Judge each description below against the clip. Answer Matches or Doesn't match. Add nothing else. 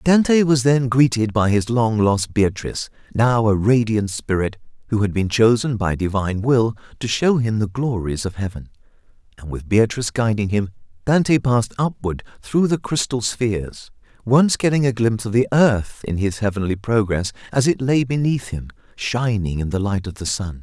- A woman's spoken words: Doesn't match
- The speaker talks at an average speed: Matches